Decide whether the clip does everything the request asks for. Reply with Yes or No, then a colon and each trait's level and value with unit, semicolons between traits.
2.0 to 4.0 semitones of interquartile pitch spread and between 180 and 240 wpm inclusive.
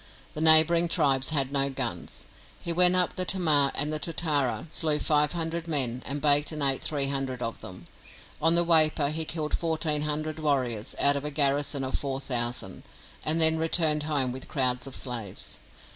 Yes: average, 2.9 semitones; average, 185 wpm